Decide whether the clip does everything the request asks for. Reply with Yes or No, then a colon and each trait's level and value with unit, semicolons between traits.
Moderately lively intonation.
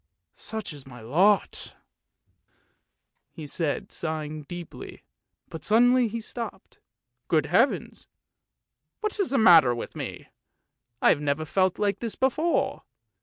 No: wide, 7.4 semitones